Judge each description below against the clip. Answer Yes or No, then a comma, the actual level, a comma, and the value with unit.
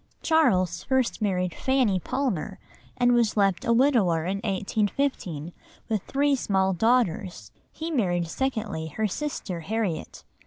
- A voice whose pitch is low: No, high, 205 Hz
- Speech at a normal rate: No, slow, 125 wpm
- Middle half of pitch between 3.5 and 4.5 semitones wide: No, wide, 5.6 semitones